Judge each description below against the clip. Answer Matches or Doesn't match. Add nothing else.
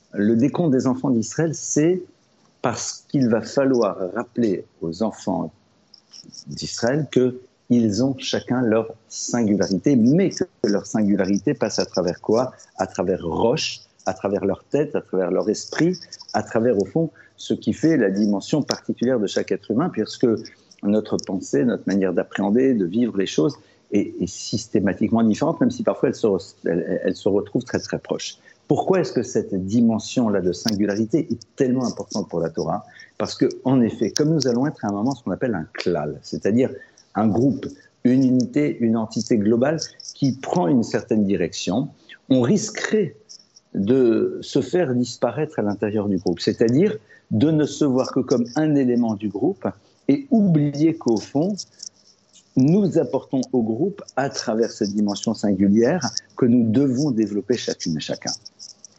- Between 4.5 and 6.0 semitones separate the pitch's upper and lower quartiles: Matches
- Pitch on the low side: Matches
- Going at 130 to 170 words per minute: Matches